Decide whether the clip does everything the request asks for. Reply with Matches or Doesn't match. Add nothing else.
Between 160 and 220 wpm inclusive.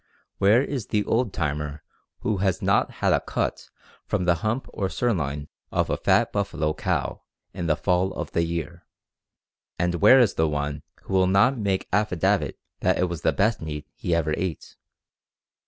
Matches